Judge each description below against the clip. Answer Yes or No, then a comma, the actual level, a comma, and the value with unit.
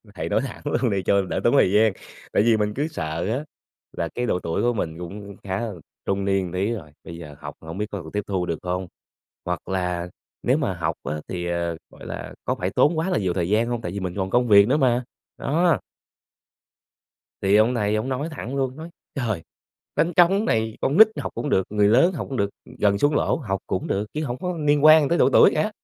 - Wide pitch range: Yes, wide, 6.5 semitones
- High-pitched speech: No, low, 105 Hz